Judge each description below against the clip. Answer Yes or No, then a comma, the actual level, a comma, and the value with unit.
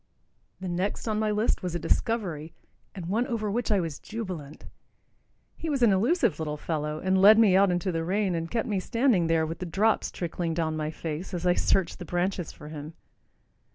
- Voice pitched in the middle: Yes, medium, 180 Hz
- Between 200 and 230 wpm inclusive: Yes, fast, 205 wpm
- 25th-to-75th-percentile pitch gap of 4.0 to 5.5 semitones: Yes, average, 4.5 semitones